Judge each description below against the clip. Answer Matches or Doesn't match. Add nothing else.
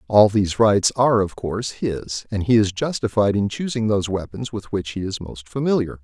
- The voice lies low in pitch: Matches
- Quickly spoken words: Matches